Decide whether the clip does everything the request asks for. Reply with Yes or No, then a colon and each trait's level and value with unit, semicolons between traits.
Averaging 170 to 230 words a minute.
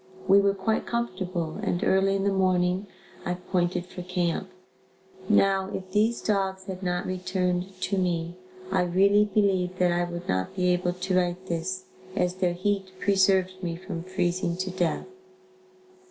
No: average, 160 wpm